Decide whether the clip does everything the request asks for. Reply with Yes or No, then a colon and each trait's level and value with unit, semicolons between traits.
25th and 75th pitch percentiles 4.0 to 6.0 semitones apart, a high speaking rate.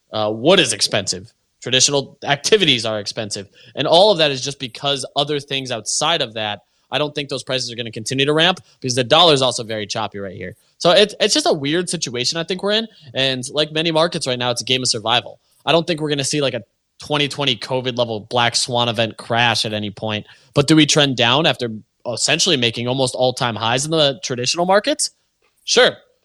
Yes: average, 4.5 semitones; fast, 225 wpm